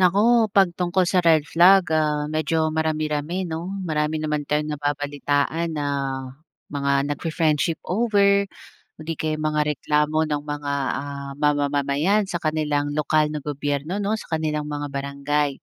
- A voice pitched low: No, medium, 150 Hz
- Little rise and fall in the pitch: Yes, narrow, 2.2 semitones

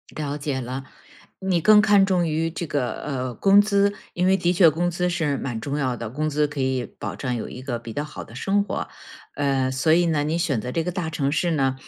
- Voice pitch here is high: No, medium, 150 Hz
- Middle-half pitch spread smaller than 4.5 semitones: No, average, 4.9 semitones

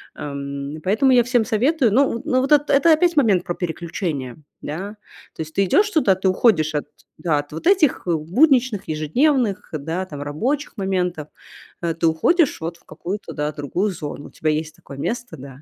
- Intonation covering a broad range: Yes, wide, 8.4 semitones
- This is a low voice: No, medium, 185 Hz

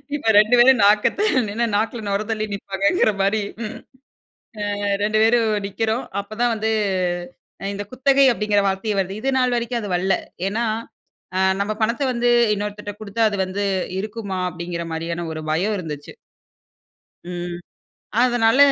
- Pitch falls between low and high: No, high, 210 Hz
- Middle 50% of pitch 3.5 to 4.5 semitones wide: No, average, 3.0 semitones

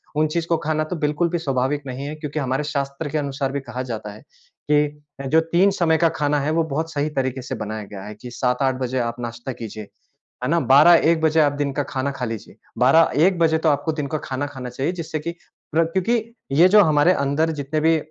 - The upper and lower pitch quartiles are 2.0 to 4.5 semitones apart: Yes, average, 3.5 semitones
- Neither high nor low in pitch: Yes, medium, 145 Hz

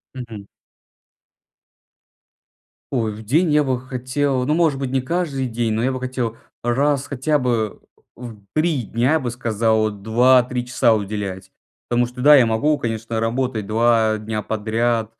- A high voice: No, low, 120 Hz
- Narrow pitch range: No, average, 3.0 semitones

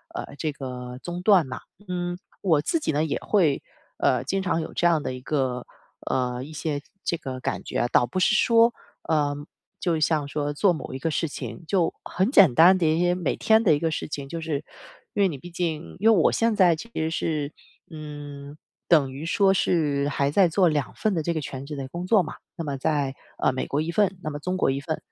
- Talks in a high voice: No, medium, 155 Hz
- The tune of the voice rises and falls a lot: No, average, 3.8 semitones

